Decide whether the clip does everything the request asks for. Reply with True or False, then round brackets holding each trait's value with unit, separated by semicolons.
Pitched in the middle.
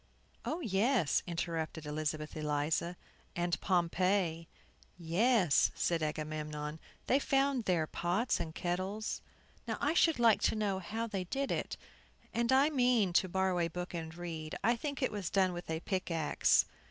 True (180 Hz)